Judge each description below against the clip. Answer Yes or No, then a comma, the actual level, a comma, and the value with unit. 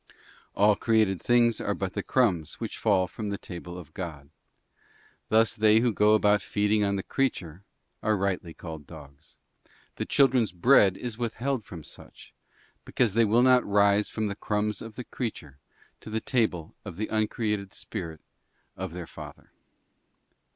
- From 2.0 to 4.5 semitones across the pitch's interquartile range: Yes, average, 3.6 semitones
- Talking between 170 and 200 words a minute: No, average, 160 wpm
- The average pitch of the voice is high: No, low, 105 Hz